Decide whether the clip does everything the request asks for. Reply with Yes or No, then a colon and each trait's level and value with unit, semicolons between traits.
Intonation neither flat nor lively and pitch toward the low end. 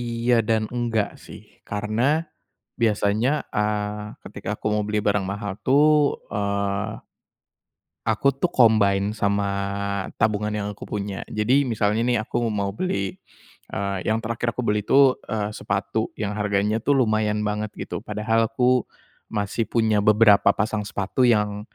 No: narrow, 1.9 semitones; low, 105 Hz